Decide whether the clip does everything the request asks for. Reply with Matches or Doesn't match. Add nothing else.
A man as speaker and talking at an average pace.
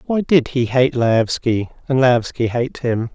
Matches